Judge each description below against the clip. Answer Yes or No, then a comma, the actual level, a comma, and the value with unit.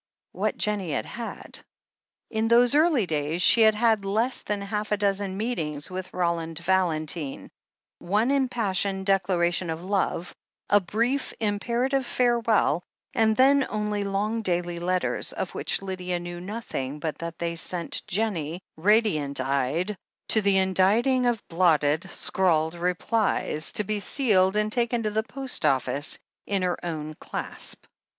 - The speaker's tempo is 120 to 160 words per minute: Yes, average, 145 wpm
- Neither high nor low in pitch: No, high, 195 Hz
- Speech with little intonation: No, average, 4.3 semitones